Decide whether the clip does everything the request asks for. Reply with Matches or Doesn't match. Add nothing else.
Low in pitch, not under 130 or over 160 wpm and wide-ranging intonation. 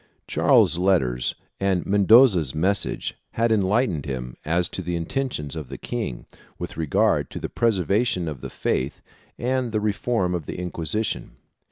Matches